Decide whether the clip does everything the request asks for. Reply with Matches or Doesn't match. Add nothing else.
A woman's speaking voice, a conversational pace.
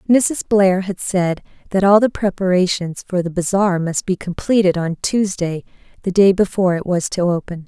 Matches